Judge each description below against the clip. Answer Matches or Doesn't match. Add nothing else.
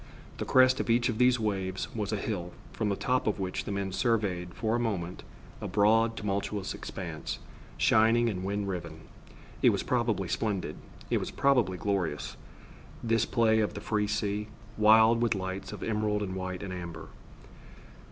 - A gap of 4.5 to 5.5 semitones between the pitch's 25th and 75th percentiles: Doesn't match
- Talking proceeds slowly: Doesn't match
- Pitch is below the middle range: Matches